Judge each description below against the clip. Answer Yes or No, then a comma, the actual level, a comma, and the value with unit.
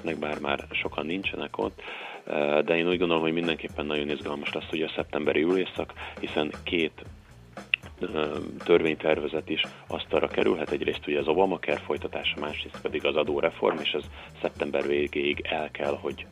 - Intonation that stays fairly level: Yes, narrow, 1.9 semitones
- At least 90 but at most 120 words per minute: No, fast, 155 wpm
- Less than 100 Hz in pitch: Yes, very low, 75 Hz